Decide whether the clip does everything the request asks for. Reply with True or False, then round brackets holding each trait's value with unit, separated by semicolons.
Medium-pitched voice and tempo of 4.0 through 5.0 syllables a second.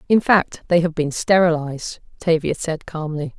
True (165 Hz; 4.7 syllables/s)